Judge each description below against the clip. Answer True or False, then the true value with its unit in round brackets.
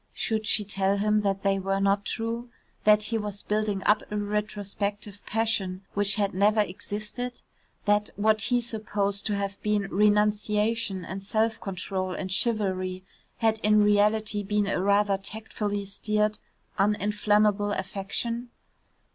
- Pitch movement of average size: False (1.3 semitones)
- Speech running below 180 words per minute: True (140 wpm)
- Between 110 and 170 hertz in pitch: False (205 Hz)